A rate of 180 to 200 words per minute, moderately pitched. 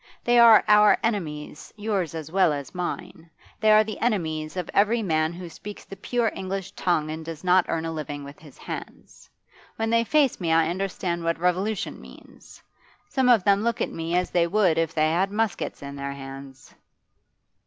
Yes: average, 190 wpm; medium, 180 Hz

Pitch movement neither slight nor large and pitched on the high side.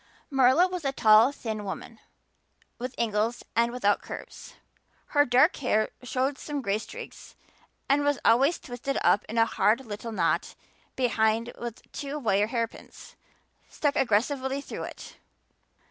Yes: average, 3.9 semitones; high, 245 Hz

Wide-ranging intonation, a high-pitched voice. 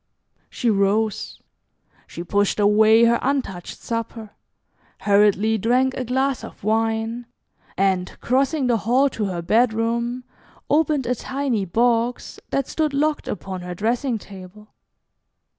No: average, 3.5 semitones; high, 225 Hz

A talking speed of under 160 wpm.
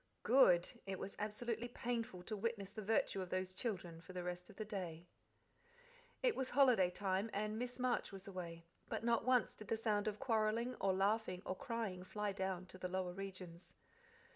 No: average, 190 wpm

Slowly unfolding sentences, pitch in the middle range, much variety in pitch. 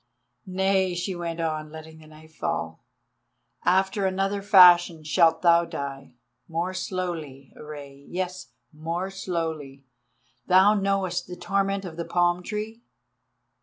No: slow, 120 wpm; medium, 175 Hz; average, 3.1 semitones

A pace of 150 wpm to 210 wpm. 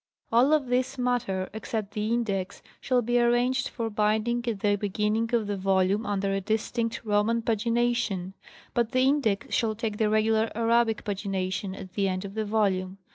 Yes: average, 180 wpm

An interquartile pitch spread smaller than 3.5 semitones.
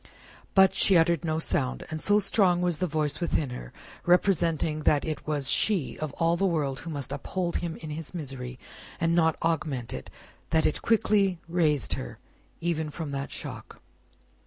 Yes: average, 3.0 semitones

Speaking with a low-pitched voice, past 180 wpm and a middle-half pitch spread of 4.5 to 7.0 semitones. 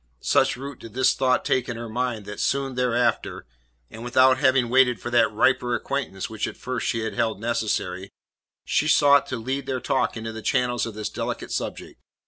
No: low, 120 Hz; average, 195 wpm; narrow, 2.6 semitones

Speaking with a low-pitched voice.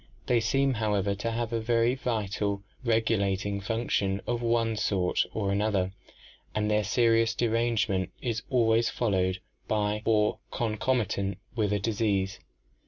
Yes: low, 110 Hz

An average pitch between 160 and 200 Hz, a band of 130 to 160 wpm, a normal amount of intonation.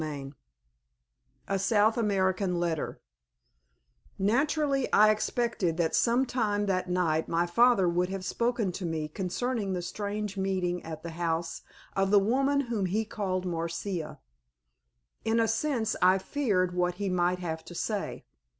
Yes: high, 190 Hz; average, 150 wpm; average, 3.9 semitones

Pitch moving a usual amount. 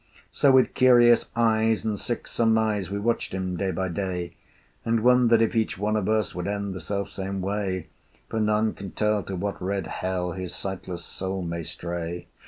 Yes: average, 3.1 semitones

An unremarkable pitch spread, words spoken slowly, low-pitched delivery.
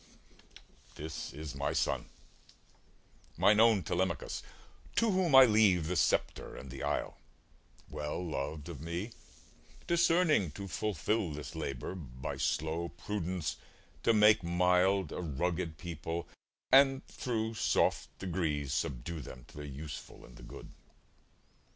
No: wide, 5.8 semitones; slow, 125 wpm; very low, 85 Hz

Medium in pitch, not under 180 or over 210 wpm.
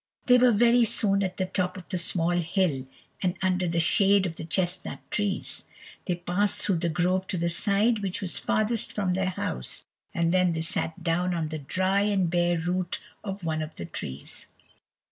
Yes: medium, 180 Hz; average, 195 wpm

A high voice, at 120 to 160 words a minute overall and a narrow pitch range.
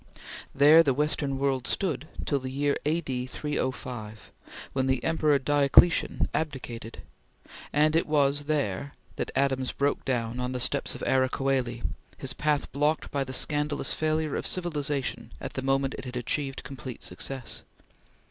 No: medium, 140 Hz; average, 150 wpm; narrow, 2.3 semitones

